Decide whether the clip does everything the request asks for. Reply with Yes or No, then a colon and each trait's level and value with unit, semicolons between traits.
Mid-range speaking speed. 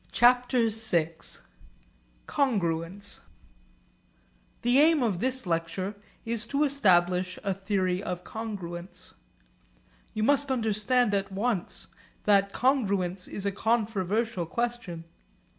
No: slow, 100 wpm